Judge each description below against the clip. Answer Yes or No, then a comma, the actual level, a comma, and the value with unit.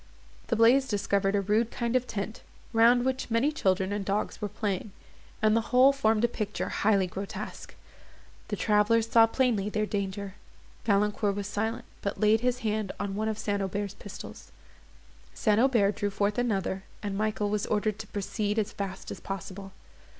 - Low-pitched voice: No, high, 210 Hz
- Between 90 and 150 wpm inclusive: No, average, 170 wpm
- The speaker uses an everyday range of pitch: No, narrow, 2.2 semitones